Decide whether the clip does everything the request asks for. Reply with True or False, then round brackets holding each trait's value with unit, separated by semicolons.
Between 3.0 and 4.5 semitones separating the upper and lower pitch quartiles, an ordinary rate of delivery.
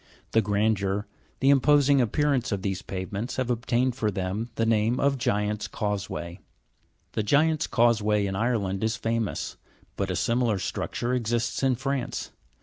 True (3.5 semitones; 155 wpm)